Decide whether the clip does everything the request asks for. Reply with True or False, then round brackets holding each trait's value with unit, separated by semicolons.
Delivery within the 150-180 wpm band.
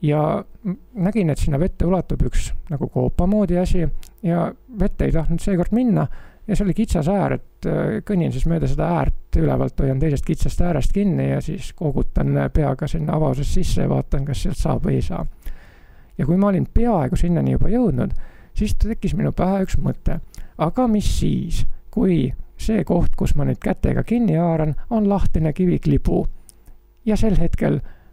True (175 wpm)